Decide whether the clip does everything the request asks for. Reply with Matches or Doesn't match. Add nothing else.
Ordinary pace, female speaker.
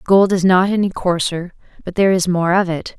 Doesn't match